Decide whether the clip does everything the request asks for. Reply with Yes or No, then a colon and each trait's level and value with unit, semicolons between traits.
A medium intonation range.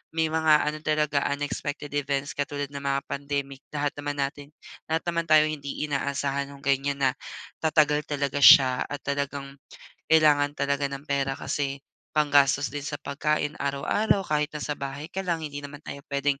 No: narrow, 1.4 semitones